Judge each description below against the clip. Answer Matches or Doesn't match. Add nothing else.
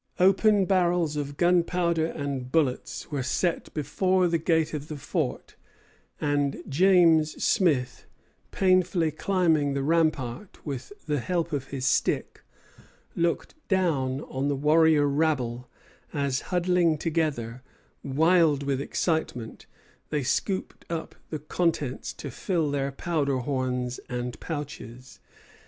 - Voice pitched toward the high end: Doesn't match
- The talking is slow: Matches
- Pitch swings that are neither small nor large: Matches